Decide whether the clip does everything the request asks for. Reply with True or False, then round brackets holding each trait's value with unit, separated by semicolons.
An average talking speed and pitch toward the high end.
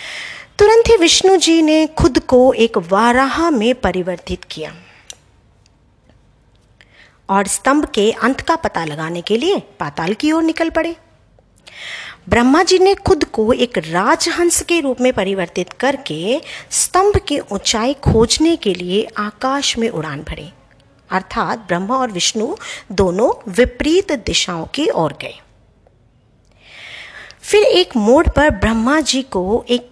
True (130 wpm; 255 Hz)